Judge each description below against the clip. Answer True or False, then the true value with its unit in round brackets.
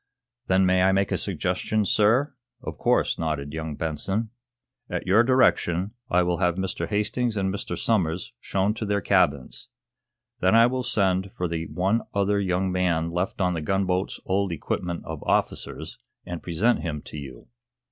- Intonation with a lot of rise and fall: False (3.2 semitones)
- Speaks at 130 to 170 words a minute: True (165 wpm)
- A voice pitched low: True (95 Hz)